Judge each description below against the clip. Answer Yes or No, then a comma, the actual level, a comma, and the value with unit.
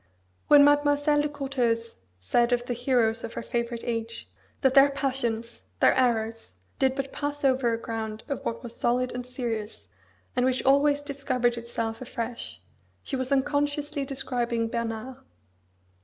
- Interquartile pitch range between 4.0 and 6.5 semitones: No, average, 3.1 semitones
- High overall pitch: Yes, very high, 250 Hz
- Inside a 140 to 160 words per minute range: Yes, average, 150 wpm